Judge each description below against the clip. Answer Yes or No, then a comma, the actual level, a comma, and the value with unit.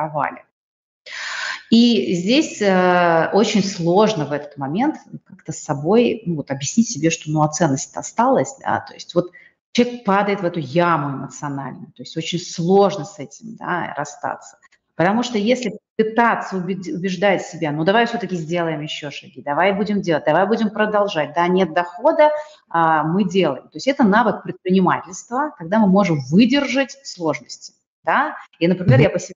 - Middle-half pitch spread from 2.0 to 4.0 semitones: No, average, 4.8 semitones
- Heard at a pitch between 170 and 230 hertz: Yes, medium, 185 Hz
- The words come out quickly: Yes, fast, 165 wpm